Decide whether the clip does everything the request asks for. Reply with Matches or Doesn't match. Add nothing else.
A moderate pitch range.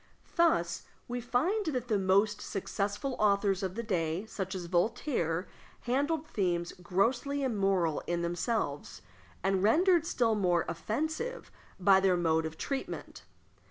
Doesn't match